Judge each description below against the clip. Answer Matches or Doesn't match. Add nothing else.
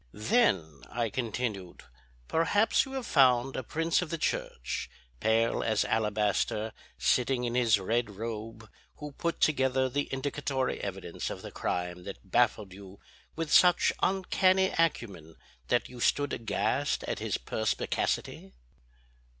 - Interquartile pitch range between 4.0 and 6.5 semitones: Matches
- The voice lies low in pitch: Matches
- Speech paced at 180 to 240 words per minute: Doesn't match